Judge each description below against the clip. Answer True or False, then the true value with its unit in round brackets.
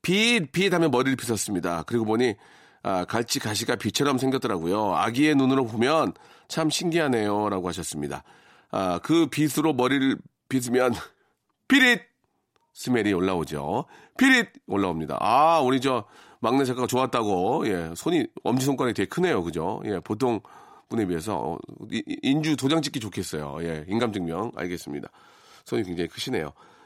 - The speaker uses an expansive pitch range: True (6.9 semitones)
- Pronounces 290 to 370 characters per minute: True (330 characters per minute)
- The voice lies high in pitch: False (130 Hz)